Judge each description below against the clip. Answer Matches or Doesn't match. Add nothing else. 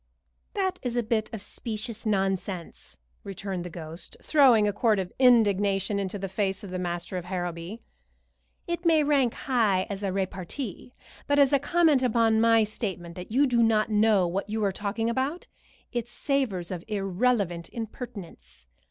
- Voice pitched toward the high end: Matches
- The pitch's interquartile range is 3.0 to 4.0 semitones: Doesn't match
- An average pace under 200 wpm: Matches